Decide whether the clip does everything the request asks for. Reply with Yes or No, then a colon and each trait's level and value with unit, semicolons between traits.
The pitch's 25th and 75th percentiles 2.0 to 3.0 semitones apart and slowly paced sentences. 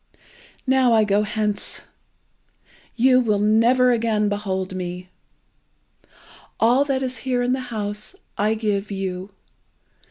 No: average, 3.5 semitones; slow, 120 wpm